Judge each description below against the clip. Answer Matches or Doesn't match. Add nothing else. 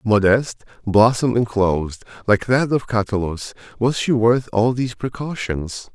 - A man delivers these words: Matches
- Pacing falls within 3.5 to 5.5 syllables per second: Matches